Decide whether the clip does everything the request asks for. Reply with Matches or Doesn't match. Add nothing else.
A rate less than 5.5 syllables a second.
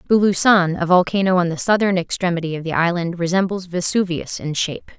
Doesn't match